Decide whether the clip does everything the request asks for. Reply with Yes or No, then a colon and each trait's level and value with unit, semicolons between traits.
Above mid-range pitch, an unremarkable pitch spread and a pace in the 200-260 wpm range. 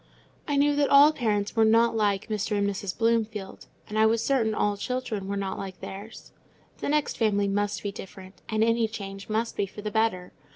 No: high, 215 Hz; narrow, 2.2 semitones; fast, 205 wpm